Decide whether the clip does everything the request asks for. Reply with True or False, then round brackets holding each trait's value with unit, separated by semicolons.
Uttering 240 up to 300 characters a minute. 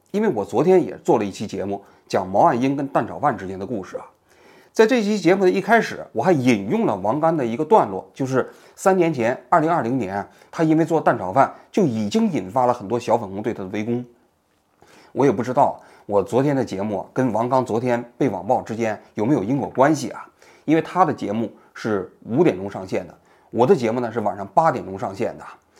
False (315 characters per minute)